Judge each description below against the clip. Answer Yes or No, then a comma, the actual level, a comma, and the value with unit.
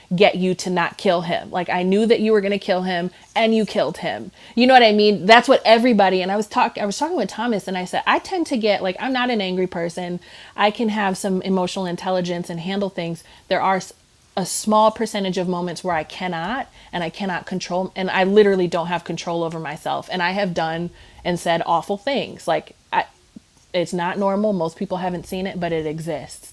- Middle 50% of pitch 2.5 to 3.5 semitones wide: Yes, average, 2.9 semitones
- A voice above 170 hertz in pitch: Yes, medium, 185 Hz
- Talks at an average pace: No, fast, 230 wpm